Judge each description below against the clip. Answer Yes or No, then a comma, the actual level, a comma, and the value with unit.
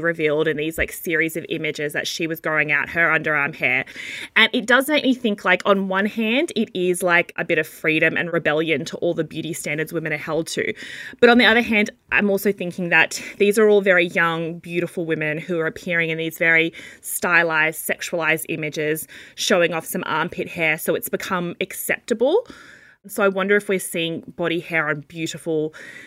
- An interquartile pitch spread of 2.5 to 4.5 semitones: Yes, average, 3.4 semitones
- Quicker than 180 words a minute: Yes, average, 200 wpm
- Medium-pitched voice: Yes, medium, 170 Hz